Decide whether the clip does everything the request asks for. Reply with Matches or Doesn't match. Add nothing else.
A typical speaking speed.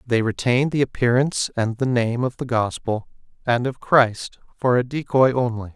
Matches